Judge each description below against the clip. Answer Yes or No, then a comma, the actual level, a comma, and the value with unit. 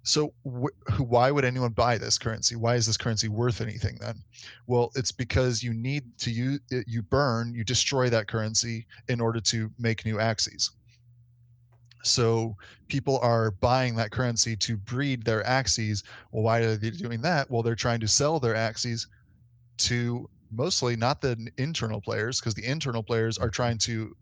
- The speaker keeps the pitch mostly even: Yes, narrow, 1.8 semitones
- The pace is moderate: Yes, average, 175 wpm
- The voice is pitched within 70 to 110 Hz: No, low, 120 Hz